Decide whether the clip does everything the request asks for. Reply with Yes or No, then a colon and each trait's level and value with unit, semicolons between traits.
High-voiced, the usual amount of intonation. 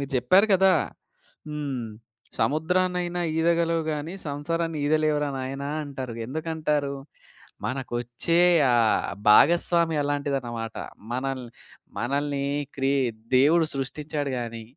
No: medium, 145 Hz; average, 3.8 semitones